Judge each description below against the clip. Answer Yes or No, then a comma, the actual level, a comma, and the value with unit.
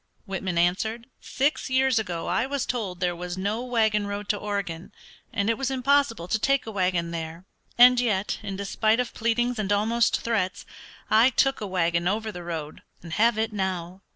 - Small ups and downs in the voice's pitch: No, average, 4.4 semitones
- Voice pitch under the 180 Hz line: No, high, 210 Hz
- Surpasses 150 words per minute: Yes, average, 185 wpm